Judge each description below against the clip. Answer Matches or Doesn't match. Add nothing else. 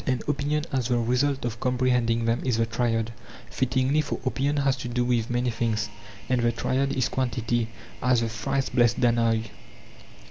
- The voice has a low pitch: Matches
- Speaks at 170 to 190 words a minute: Matches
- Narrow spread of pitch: Matches